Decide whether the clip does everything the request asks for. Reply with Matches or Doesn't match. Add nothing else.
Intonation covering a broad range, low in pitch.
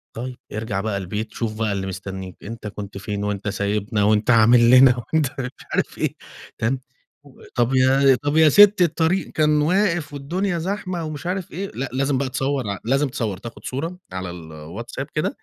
Matches